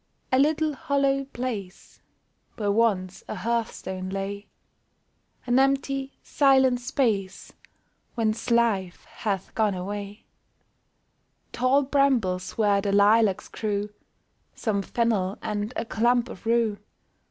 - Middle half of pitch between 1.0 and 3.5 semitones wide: No, average, 4.2 semitones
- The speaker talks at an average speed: No, slow, 105 wpm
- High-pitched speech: Yes, high, 220 Hz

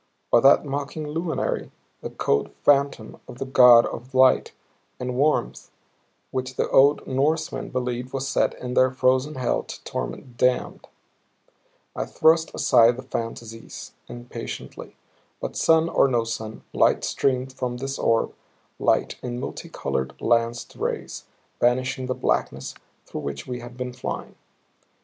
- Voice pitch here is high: No, low, 125 Hz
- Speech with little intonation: Yes, narrow, 2.1 semitones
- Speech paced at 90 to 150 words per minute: Yes, average, 140 wpm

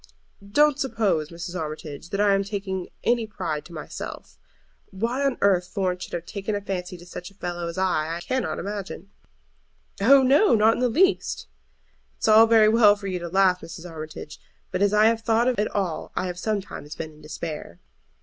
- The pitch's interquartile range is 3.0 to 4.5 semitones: Yes, average, 4.1 semitones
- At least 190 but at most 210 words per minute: Yes, average, 200 wpm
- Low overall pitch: No, high, 195 Hz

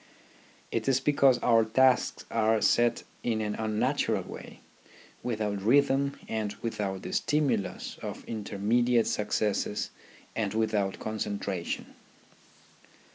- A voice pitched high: No, low, 110 Hz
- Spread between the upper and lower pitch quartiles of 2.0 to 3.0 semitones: Yes, average, 2.7 semitones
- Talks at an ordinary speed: No, slow, 105 wpm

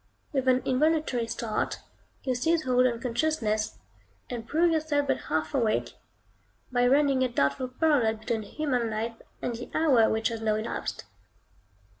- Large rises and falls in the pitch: No, average, 4.2 semitones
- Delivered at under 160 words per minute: Yes, average, 150 wpm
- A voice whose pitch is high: Yes, very high, 250 Hz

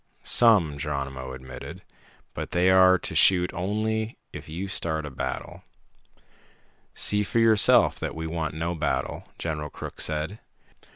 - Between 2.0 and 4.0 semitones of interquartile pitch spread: No, average, 4.5 semitones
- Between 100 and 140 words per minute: Yes, slow, 135 wpm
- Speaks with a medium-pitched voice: No, very low, 85 Hz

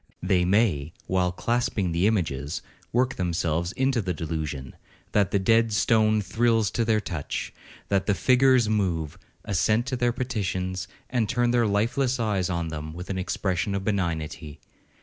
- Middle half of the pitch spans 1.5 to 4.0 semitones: No, average, 4.9 semitones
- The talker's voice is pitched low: Yes, low, 100 Hz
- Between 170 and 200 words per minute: No, average, 155 wpm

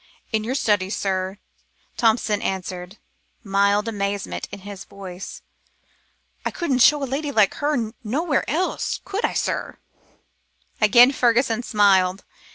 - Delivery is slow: Yes, slow, 125 wpm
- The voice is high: Yes, high, 215 Hz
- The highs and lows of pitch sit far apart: No, average, 4.5 semitones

